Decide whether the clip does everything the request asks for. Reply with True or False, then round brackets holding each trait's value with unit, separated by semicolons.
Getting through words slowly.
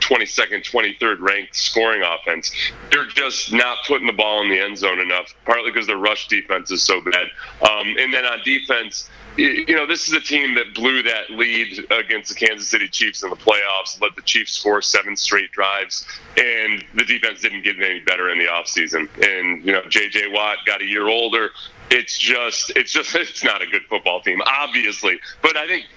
False (200 wpm)